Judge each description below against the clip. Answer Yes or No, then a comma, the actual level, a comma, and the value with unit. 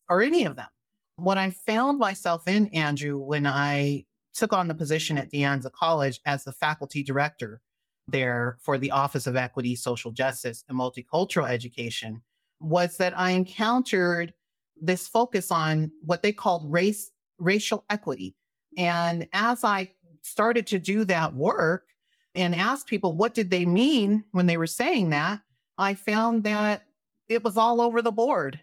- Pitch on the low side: No, medium, 175 Hz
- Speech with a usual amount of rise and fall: No, wide, 6.7 semitones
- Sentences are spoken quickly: No, average, 160 wpm